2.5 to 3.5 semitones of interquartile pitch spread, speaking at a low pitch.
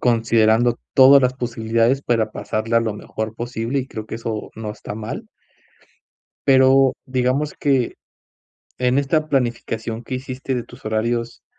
Yes: average, 2.8 semitones; low, 120 Hz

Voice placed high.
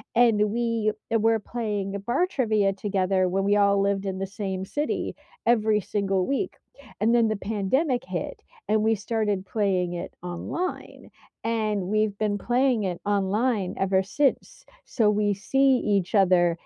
Yes: high, 210 Hz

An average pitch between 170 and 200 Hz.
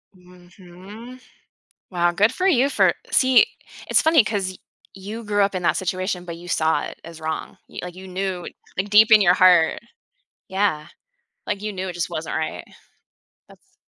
Yes: medium, 185 Hz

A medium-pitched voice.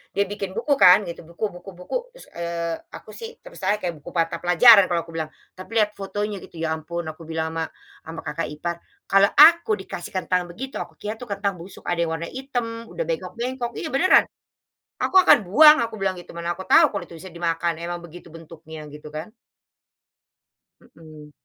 Yes: medium, 180 Hz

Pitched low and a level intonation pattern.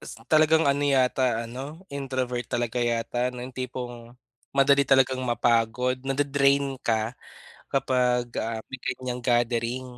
Yes: low, 125 Hz; narrow, 2.1 semitones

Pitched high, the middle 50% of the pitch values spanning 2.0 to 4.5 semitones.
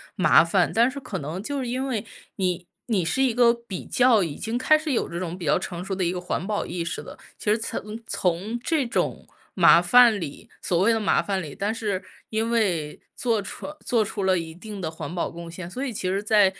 No: high, 200 Hz; average, 4.9 semitones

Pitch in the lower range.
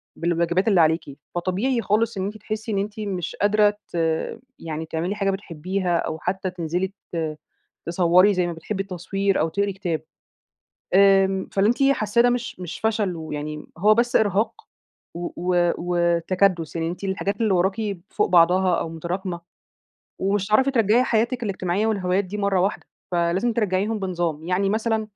No: high, 190 Hz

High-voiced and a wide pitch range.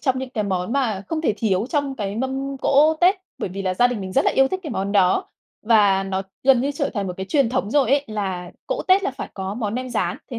Yes: high, 235 Hz; wide, 5.8 semitones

